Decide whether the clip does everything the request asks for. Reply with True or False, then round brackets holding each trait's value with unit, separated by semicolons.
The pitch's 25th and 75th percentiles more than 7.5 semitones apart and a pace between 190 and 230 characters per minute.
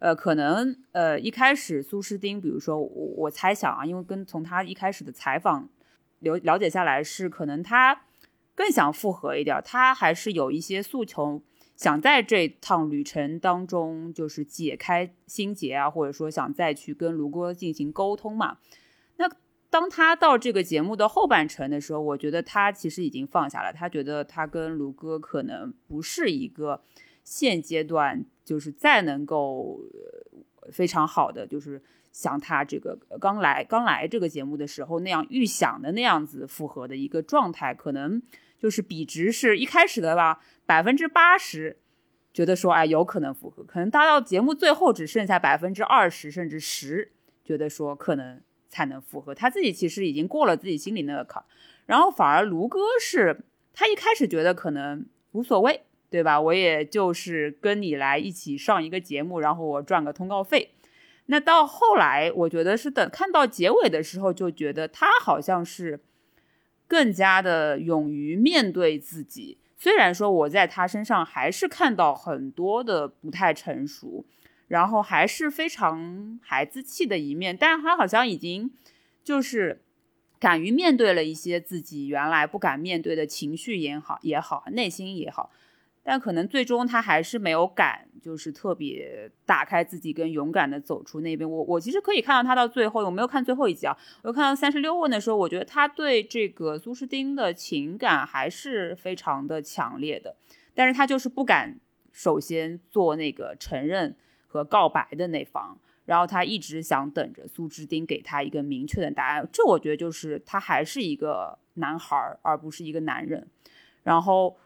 False (8.6 semitones; 270 characters per minute)